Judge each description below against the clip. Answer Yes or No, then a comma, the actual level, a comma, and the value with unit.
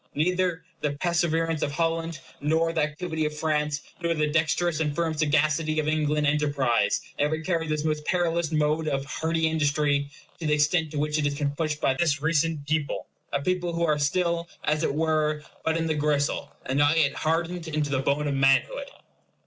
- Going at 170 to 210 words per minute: Yes, average, 190 wpm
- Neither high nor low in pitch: Yes, medium, 155 Hz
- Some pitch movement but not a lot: No, narrow, 1.8 semitones